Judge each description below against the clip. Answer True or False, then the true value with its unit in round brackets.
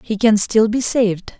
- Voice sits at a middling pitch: False (215 Hz)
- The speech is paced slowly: False (215 wpm)